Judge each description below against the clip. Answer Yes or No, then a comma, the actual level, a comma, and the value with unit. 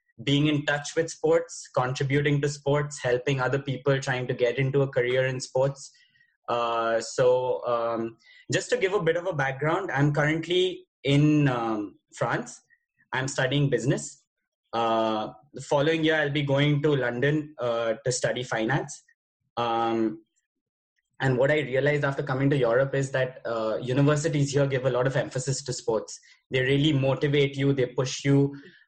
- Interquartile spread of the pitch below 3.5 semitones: Yes, average, 2.9 semitones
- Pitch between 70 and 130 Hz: No, medium, 140 Hz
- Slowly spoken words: No, average, 165 wpm